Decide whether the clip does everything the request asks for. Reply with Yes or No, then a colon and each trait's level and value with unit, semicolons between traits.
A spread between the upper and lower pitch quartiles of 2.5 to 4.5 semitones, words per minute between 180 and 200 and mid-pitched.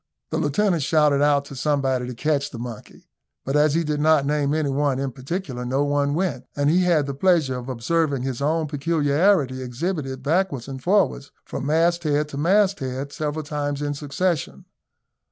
Yes: average, 2.8 semitones; average, 185 wpm; medium, 145 Hz